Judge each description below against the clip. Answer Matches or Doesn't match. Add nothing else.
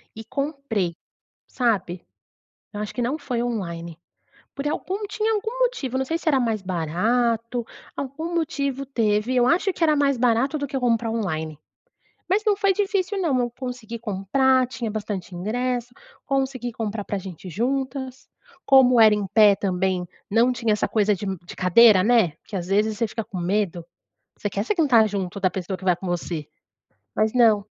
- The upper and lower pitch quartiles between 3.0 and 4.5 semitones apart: Doesn't match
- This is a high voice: Matches